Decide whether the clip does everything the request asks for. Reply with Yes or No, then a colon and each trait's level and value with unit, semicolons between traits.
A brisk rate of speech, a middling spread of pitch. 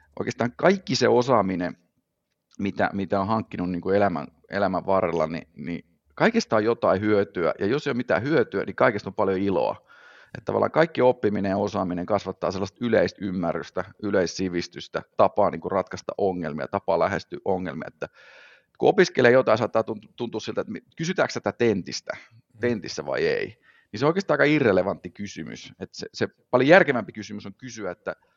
Yes: fast, 165 wpm; average, 3.6 semitones